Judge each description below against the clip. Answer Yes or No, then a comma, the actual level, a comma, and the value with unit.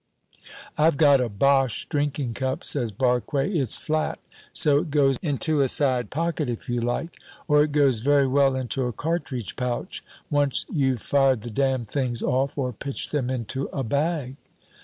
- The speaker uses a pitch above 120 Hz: Yes, low, 135 Hz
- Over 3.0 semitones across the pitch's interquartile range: No, narrow, 2.6 semitones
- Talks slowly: No, average, 170 wpm